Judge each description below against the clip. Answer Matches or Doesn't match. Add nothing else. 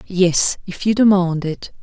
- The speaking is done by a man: Doesn't match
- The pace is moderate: Matches